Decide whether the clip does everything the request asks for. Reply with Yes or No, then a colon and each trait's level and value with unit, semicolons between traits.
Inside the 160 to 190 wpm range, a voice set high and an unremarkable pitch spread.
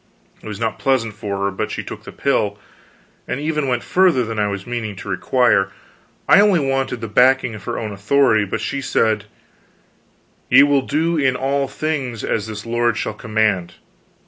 No: average, 185 wpm; low, 120 Hz; average, 4.3 semitones